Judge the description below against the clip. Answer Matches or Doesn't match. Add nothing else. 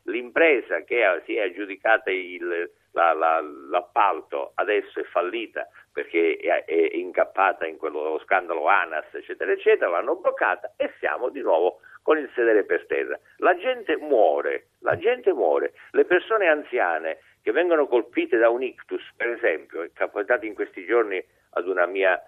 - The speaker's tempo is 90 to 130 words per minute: Doesn't match